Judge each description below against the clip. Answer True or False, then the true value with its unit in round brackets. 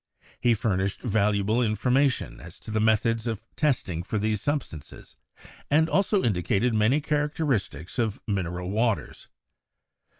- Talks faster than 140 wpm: False (135 wpm)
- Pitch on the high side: False (110 Hz)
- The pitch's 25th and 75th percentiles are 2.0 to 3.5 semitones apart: False (4.2 semitones)